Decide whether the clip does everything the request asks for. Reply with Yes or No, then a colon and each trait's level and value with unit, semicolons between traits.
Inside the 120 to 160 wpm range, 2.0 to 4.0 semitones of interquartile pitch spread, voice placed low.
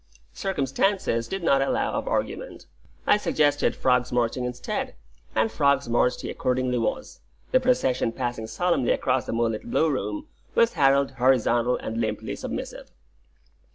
No: average, 140 wpm; average, 4.5 semitones; low, 130 Hz